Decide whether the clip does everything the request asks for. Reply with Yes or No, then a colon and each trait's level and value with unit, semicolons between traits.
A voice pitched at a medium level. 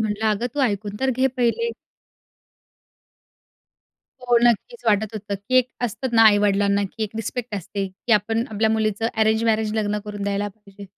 No: high, 215 Hz